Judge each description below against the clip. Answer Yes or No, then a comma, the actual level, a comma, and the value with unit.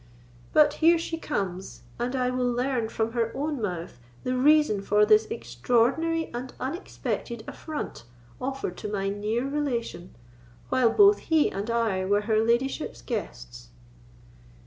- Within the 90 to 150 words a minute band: Yes, average, 140 wpm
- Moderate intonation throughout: Yes, average, 4.9 semitones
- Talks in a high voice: Yes, high, 235 Hz